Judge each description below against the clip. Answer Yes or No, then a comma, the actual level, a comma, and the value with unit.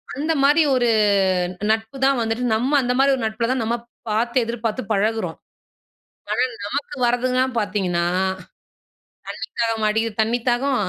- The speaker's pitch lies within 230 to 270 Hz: Yes, high, 235 Hz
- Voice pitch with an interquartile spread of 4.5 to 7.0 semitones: No, average, 2.7 semitones